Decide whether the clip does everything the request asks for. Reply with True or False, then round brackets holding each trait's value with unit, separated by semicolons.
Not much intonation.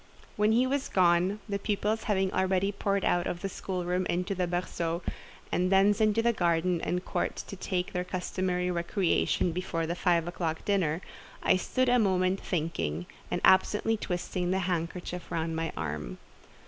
True (2.2 semitones)